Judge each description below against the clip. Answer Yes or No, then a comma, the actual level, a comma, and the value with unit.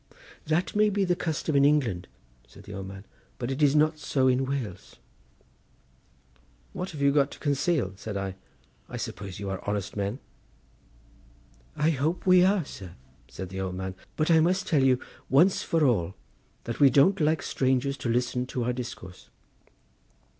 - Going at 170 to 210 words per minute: Yes, average, 175 wpm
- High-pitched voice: No, low, 135 Hz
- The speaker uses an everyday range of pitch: No, wide, 7.3 semitones